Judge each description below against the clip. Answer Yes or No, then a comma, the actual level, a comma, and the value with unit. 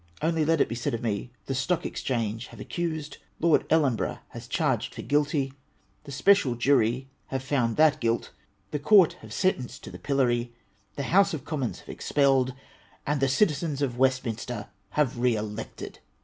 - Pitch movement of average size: Yes, average, 4.1 semitones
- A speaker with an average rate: Yes, average, 175 wpm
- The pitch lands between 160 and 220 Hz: No, low, 135 Hz